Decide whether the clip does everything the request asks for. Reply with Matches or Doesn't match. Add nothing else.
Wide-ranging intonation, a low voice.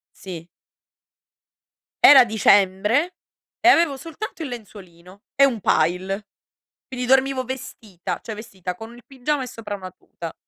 Doesn't match